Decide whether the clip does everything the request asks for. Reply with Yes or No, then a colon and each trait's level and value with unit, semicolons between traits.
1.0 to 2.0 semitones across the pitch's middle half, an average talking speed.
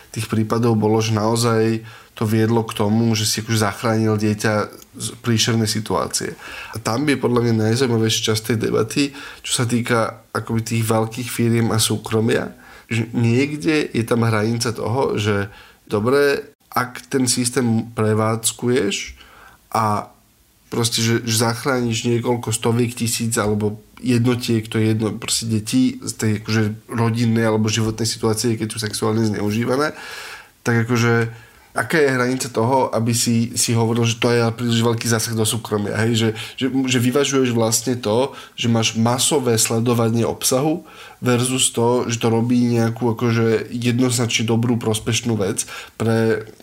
Yes: narrow, 1.5 semitones; average, 145 wpm